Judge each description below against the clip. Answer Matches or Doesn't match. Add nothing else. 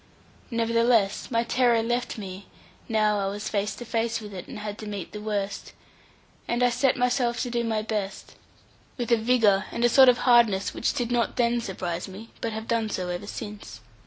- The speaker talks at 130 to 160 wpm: Doesn't match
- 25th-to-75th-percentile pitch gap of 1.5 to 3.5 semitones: Matches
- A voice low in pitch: Doesn't match